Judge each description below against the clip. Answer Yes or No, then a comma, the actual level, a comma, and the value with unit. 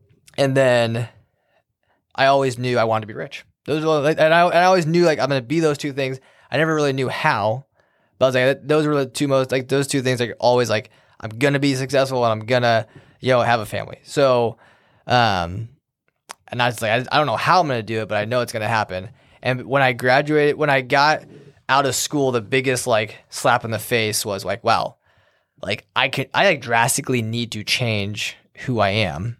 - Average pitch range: Yes, average, 3.4 semitones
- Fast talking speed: Yes, fast, 235 wpm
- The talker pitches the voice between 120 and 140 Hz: Yes, low, 130 Hz